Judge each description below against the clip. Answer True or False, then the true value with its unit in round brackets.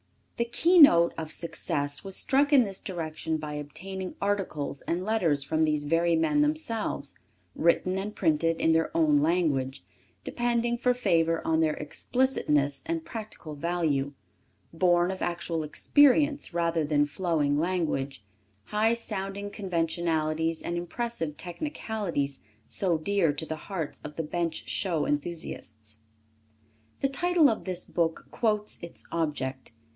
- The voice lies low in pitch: False (170 Hz)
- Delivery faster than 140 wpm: False (135 wpm)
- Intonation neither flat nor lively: True (5.0 semitones)